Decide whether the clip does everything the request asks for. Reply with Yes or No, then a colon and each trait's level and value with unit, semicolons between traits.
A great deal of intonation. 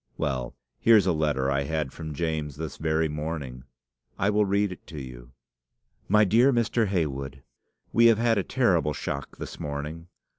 Yes: wide, 6.3 semitones